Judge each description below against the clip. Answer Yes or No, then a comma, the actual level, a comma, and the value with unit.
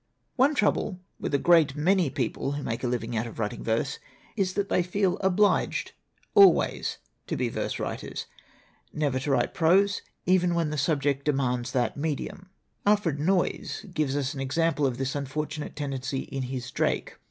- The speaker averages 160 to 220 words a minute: Yes, average, 170 wpm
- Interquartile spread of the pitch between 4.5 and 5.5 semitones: Yes, average, 5.1 semitones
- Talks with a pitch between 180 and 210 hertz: No, medium, 145 Hz